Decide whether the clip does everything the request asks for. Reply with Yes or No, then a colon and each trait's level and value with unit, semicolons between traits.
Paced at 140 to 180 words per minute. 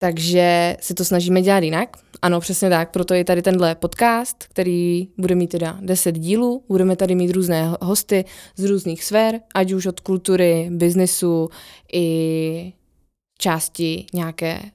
Yes: average, 145 wpm